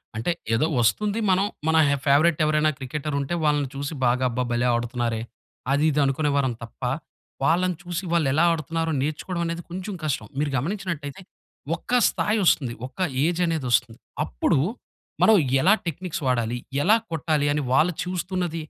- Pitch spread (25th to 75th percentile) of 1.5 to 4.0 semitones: No, average, 4.6 semitones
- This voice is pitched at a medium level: Yes, medium, 155 Hz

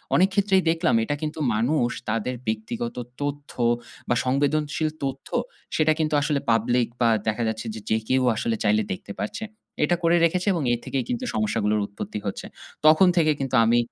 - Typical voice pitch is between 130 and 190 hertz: Yes, low, 135 Hz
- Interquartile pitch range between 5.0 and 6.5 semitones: Yes, wide, 5.5 semitones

